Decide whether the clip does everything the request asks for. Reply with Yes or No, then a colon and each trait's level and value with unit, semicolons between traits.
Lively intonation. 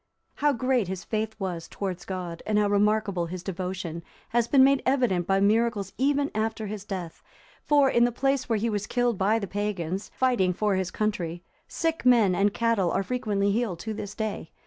No: average, 3.9 semitones